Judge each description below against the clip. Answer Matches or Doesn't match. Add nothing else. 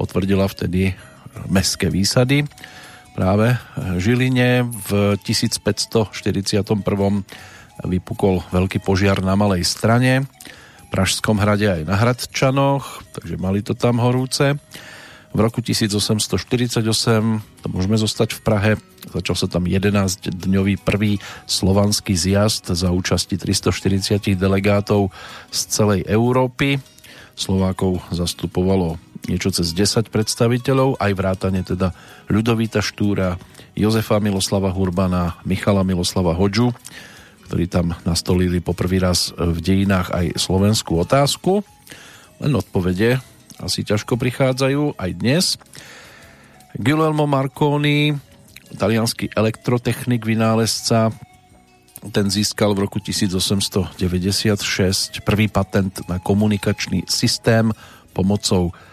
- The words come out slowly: Matches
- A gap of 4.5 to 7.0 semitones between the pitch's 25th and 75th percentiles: Doesn't match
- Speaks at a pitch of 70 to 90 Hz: Doesn't match